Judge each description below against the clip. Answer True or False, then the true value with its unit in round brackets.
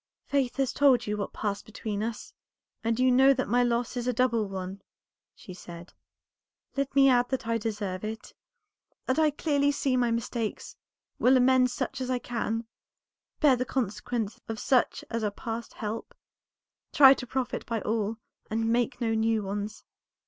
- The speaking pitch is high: True (235 Hz)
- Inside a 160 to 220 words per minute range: True (175 wpm)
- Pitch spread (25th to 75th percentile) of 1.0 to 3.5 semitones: True (2.9 semitones)